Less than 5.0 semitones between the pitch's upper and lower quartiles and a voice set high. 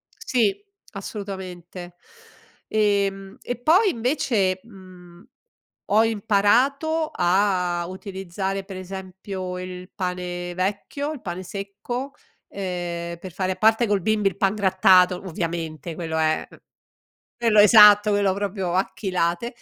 Yes: narrow, 2.6 semitones; high, 195 Hz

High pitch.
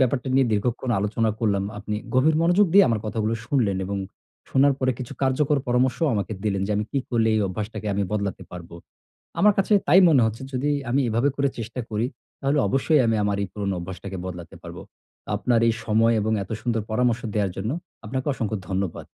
No: low, 115 Hz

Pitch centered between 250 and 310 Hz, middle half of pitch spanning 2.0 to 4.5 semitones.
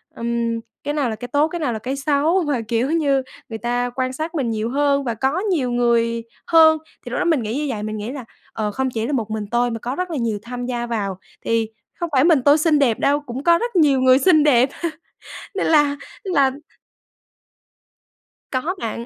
Yes: very high, 260 Hz; average, 4.2 semitones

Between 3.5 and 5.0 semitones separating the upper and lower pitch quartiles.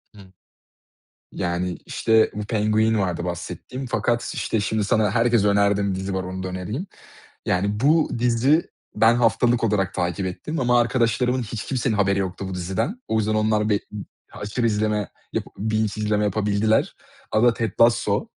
No: average, 2.9 semitones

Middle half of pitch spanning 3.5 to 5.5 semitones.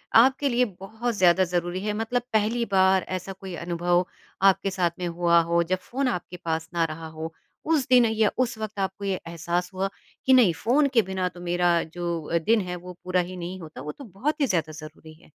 Yes: average, 4.4 semitones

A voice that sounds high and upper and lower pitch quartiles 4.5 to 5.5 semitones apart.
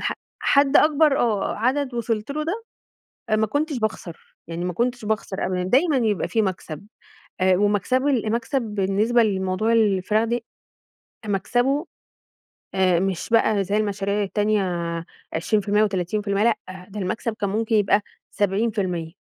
No: high, 210 Hz; average, 3.5 semitones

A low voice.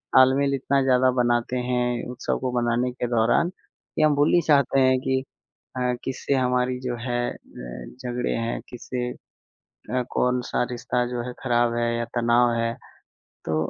Yes: low, 125 Hz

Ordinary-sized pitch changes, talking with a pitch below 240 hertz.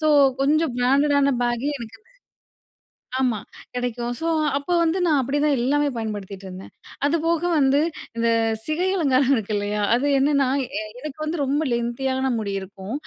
No: average, 3.8 semitones; very high, 265 Hz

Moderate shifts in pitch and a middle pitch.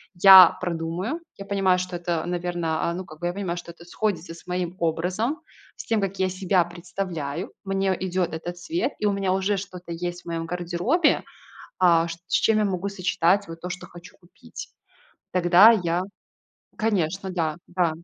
No: narrow, 2.2 semitones; medium, 180 Hz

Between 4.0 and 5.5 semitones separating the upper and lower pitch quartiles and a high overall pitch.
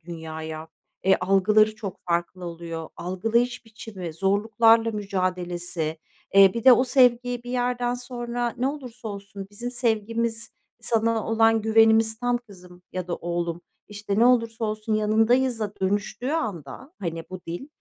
Yes: average, 4.5 semitones; high, 215 Hz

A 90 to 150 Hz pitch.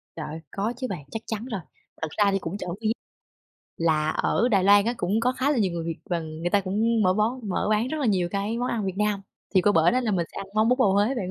No: high, 205 Hz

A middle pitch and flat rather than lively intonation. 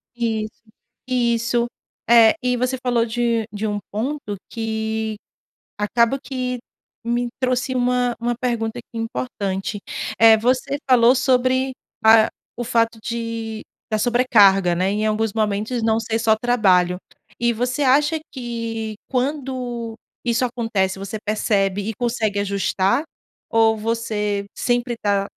No: high, 230 Hz; narrow, 2.3 semitones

